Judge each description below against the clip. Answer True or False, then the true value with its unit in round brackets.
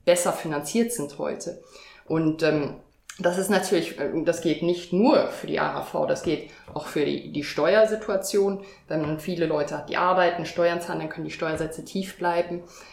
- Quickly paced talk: False (175 wpm)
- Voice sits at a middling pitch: True (175 Hz)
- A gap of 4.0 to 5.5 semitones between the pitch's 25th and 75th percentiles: False (3.3 semitones)